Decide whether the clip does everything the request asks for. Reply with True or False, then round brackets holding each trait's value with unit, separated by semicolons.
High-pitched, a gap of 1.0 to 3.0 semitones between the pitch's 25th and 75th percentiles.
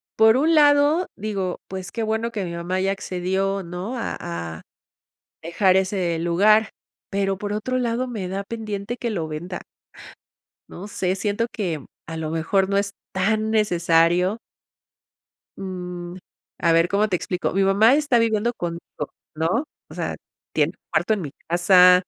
False (195 Hz; 3.6 semitones)